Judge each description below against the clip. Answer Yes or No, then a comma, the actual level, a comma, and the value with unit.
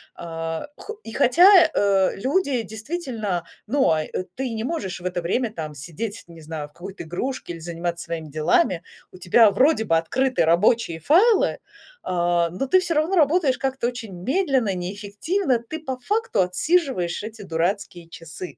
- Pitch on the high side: Yes, high, 205 Hz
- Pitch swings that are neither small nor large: No, wide, 7.6 semitones